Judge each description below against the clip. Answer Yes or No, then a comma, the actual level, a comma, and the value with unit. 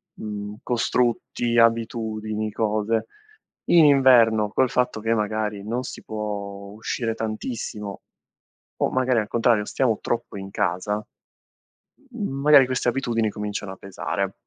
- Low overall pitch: Yes, low, 110 Hz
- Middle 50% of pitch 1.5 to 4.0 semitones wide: Yes, narrow, 2.6 semitones